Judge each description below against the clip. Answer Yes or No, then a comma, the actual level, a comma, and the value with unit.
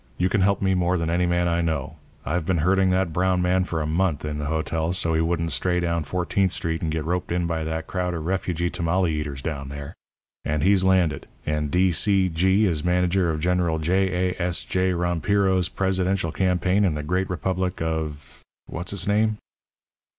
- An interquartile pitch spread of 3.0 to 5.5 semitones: No, narrow, 2.5 semitones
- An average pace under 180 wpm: No, average, 200 wpm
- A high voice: No, very low, 90 Hz